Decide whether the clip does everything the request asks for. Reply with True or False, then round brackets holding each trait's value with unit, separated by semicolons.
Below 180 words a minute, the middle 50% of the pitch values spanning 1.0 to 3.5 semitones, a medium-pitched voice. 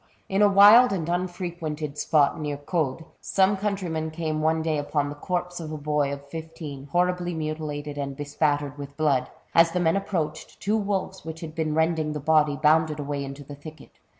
False (185 wpm; 3.1 semitones; 155 Hz)